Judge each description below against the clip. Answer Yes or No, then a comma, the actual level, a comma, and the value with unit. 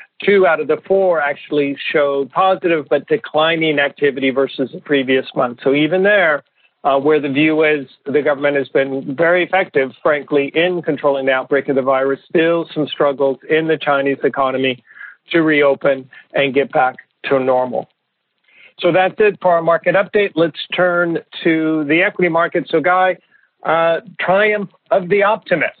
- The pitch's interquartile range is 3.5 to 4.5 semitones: Yes, average, 4.1 semitones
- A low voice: No, medium, 155 Hz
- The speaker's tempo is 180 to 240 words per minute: No, average, 165 wpm